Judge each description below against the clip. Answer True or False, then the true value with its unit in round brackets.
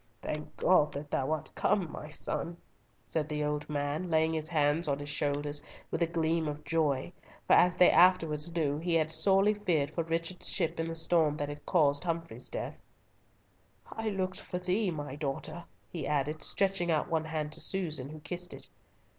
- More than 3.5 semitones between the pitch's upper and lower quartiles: False (2.7 semitones)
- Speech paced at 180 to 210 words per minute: True (190 wpm)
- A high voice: False (160 Hz)